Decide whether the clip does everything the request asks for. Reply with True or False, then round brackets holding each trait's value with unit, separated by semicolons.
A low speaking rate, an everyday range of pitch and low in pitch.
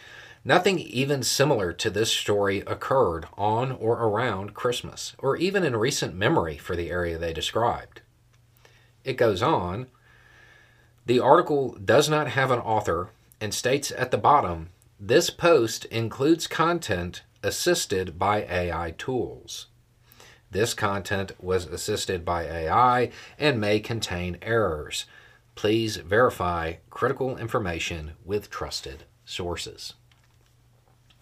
True (115 wpm; 4.4 semitones; 115 Hz)